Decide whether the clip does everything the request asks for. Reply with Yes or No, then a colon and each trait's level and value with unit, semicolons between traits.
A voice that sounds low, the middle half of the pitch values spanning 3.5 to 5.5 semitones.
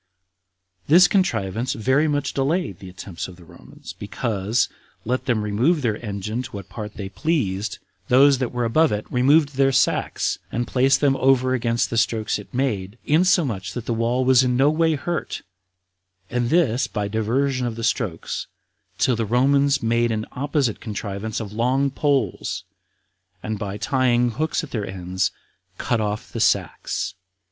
Yes: low, 120 Hz; average, 4.3 semitones